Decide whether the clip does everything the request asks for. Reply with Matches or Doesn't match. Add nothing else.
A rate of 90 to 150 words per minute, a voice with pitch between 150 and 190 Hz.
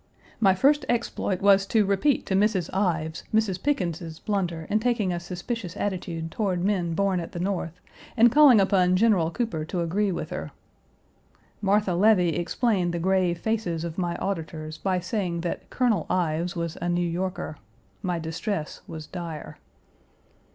Doesn't match